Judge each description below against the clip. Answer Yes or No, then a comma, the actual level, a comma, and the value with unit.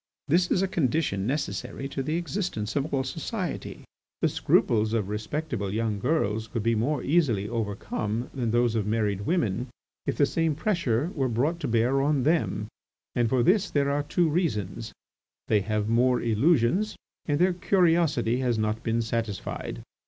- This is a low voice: Yes, low, 125 Hz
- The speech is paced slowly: No, average, 165 wpm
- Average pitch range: No, wide, 6.2 semitones